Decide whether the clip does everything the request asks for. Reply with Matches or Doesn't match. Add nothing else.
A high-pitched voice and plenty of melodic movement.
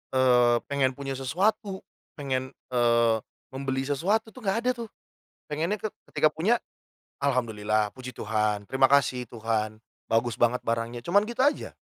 Doesn't match